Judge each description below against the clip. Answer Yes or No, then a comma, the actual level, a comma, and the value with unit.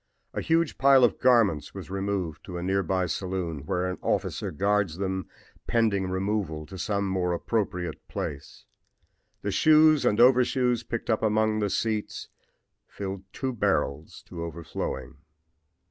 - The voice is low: Yes, low, 100 Hz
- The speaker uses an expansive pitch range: No, average, 4.1 semitones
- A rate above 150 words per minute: No, average, 145 wpm